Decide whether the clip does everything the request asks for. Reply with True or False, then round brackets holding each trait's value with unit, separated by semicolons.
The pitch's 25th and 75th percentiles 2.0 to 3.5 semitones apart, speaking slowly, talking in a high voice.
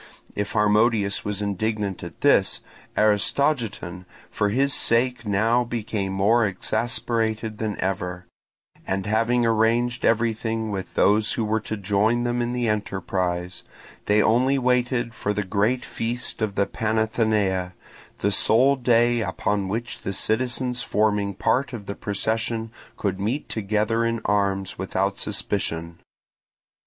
False (2.9 semitones; 130 wpm; 110 Hz)